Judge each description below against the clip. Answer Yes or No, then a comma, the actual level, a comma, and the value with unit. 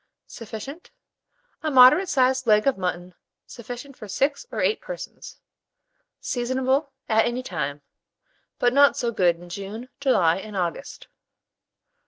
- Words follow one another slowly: Yes, slow, 130 wpm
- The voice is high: Yes, high, 240 Hz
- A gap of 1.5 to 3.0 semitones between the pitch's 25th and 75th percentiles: No, wide, 5.6 semitones